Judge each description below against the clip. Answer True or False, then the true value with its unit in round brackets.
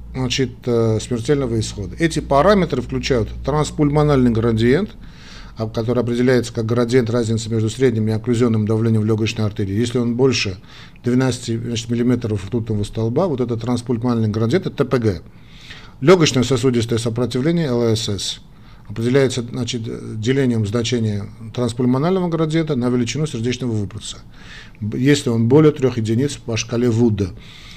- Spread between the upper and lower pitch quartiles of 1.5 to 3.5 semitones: True (2.7 semitones)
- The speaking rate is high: False (120 wpm)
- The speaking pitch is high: False (120 Hz)